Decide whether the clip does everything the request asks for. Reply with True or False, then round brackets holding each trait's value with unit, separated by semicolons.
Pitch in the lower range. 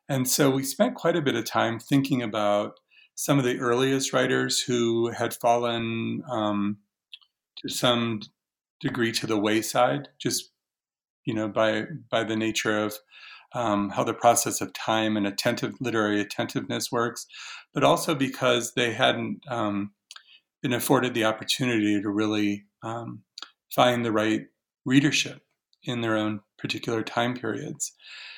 True (115 Hz)